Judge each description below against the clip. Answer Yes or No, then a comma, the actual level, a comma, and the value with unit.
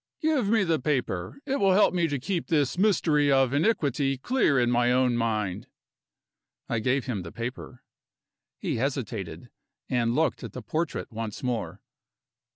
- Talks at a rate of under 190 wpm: Yes, average, 160 wpm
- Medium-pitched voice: No, low, 130 Hz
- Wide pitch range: Yes, wide, 5.8 semitones